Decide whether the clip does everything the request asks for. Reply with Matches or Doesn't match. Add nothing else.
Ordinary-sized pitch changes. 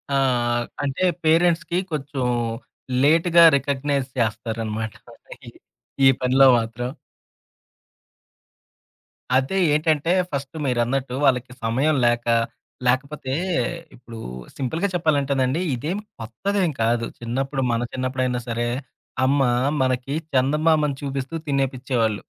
Matches